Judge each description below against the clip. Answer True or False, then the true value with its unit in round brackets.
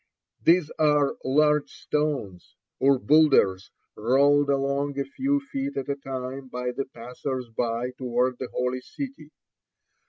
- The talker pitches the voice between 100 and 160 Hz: True (135 Hz)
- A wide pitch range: False (2.9 semitones)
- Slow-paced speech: True (130 wpm)